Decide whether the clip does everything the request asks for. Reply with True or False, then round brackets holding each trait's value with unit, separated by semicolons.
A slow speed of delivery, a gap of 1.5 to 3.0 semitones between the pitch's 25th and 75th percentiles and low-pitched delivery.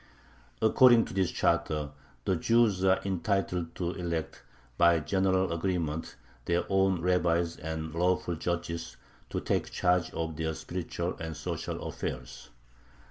True (130 wpm; 2.4 semitones; 85 Hz)